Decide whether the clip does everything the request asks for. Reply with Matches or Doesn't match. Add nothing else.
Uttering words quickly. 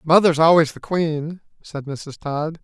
Doesn't match